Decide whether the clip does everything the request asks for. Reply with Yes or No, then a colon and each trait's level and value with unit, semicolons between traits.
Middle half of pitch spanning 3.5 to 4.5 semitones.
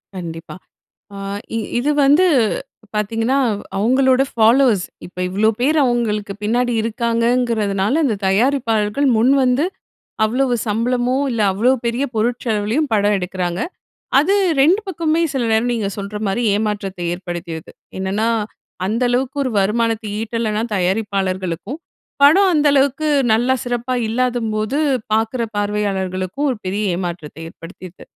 Yes: average, 4.1 semitones